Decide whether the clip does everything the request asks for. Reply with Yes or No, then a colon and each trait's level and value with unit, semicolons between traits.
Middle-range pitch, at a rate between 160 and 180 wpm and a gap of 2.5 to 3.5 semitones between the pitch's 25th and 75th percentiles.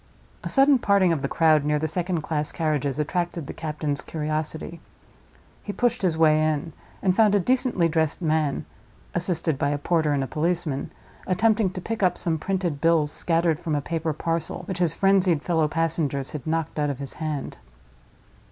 Yes: medium, 160 Hz; average, 175 wpm; average, 2.9 semitones